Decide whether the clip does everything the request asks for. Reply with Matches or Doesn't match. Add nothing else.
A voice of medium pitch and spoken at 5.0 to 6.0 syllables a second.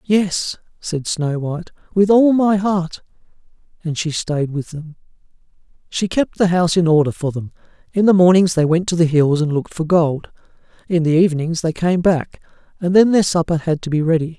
Matches